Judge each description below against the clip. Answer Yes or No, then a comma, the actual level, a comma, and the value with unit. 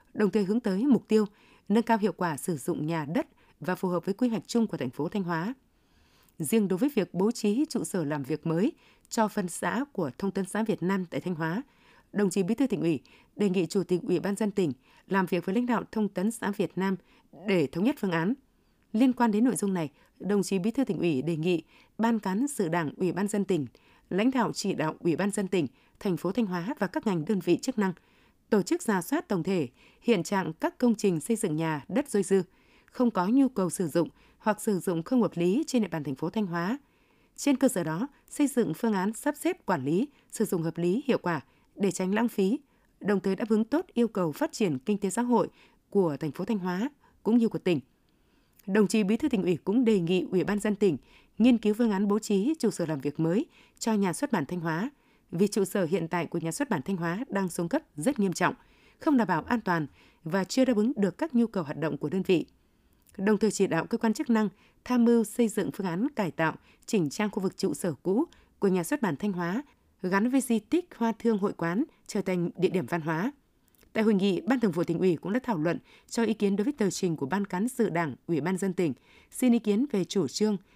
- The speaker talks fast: Yes, fast, 255 wpm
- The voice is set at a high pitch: Yes, high, 200 Hz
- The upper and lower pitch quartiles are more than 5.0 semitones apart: No, average, 4.5 semitones